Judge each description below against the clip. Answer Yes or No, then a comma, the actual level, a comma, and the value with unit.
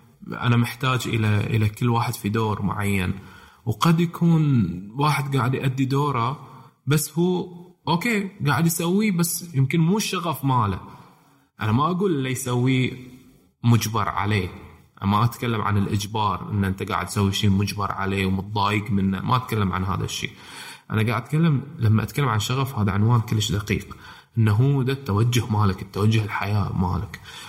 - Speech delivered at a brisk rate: Yes, fast, 155 wpm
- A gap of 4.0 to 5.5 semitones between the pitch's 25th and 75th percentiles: Yes, average, 5.1 semitones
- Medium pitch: No, low, 115 Hz